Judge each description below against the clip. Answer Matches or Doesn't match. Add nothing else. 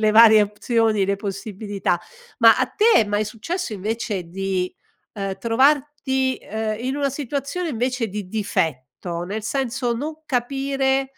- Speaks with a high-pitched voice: Matches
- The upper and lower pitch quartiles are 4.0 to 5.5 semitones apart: Matches